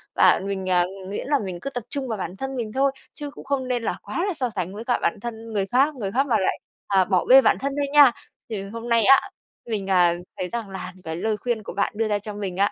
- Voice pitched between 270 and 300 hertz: No, high, 220 Hz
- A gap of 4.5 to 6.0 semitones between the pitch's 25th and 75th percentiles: Yes, average, 5.1 semitones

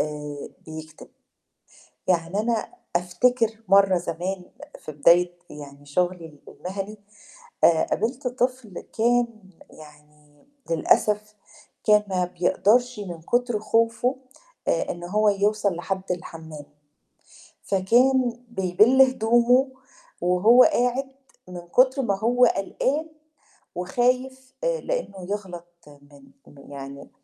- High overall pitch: Yes, high, 200 Hz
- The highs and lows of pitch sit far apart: Yes, wide, 5.9 semitones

